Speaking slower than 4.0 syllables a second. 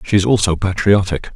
No: 5.6 syllables/s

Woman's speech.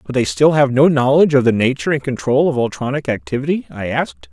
No: male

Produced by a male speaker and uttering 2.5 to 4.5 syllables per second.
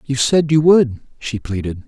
Yes: male; 4.4 syllables/s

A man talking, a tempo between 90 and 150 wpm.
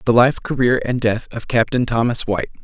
No: male; fast, 205 wpm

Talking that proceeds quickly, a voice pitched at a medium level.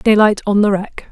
No: fast, 215 wpm; high, 205 Hz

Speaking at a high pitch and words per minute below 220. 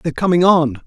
No: medium, 160 Hz; fast, 210 wpm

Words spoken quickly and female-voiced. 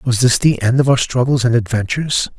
No: fast, 225 wpm; male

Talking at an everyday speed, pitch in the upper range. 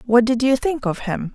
No: fast, 270 wpm; high, 240 Hz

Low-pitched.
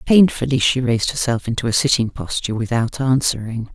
Yes: low, 125 Hz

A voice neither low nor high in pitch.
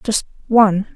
No: high, 210 Hz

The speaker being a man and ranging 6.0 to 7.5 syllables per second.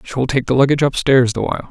Yes: male; 6.8 syllables/s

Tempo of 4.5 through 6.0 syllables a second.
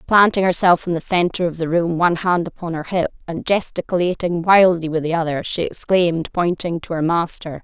Yes: 5.5 syllables/s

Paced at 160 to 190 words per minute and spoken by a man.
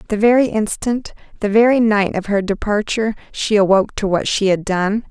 No: average, 175 wpm; female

